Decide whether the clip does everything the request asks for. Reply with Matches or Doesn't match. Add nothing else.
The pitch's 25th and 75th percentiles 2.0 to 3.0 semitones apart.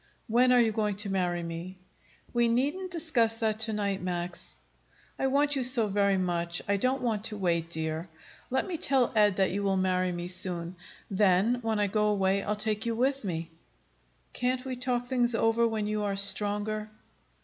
Doesn't match